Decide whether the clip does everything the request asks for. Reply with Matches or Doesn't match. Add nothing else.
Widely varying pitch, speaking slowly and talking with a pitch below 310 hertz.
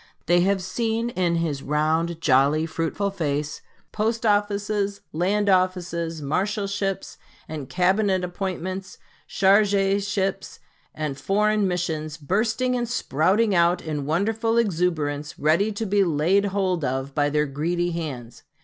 Doesn't match